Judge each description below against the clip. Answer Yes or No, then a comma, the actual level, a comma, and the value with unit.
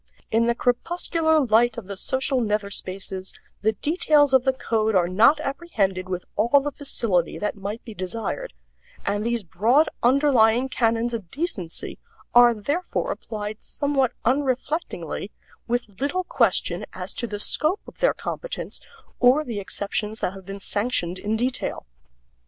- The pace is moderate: Yes, average, 150 wpm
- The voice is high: Yes, high, 230 Hz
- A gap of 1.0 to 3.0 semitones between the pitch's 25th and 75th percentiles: No, average, 5.1 semitones